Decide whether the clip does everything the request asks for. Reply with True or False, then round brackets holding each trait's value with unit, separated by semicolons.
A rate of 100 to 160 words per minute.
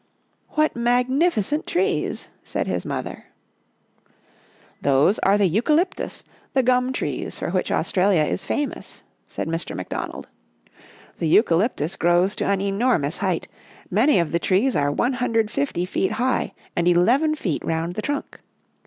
True (145 wpm)